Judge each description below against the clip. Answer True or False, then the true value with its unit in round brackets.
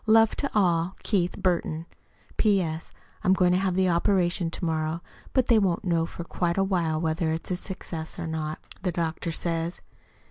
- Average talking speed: True (175 wpm)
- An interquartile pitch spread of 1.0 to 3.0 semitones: True (2.5 semitones)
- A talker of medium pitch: True (175 Hz)